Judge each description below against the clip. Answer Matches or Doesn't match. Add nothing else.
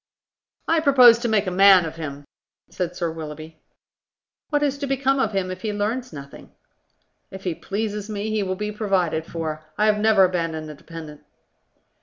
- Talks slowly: Doesn't match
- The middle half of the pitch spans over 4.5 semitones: Matches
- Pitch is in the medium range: Doesn't match